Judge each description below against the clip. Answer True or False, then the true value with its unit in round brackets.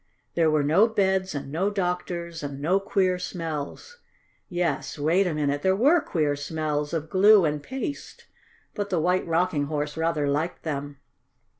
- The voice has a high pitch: False (165 Hz)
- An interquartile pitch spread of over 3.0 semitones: True (4.2 semitones)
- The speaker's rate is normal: True (160 wpm)